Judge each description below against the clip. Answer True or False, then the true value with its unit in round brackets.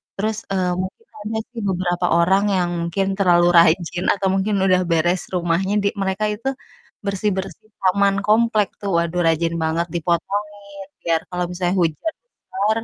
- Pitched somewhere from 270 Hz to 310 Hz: False (185 Hz)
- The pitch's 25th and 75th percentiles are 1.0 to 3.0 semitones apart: True (2.7 semitones)